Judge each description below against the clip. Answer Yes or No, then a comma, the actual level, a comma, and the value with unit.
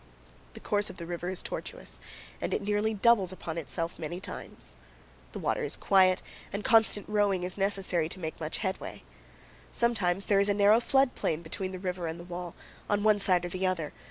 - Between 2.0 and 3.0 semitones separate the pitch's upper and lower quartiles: Yes, average, 2.7 semitones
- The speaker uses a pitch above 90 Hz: Yes, medium, 185 Hz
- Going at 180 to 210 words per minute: Yes, average, 200 wpm